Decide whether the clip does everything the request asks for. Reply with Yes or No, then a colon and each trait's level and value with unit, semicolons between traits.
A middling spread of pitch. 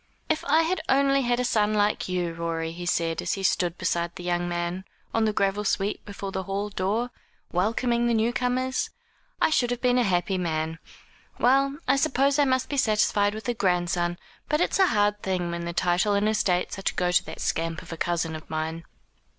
No: wide, 5.7 semitones